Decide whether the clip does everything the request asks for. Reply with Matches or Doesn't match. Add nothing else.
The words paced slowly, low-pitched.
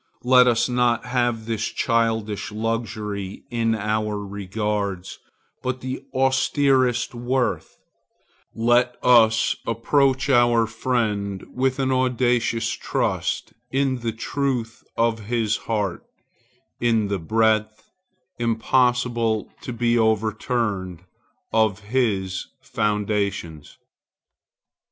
Matches